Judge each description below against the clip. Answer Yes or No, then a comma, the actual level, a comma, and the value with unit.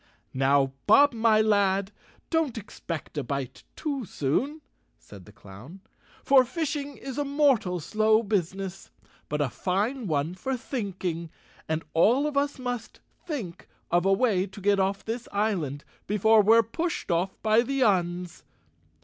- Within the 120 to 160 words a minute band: Yes, average, 150 wpm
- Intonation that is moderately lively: No, wide, 6.4 semitones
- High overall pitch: Yes, high, 205 Hz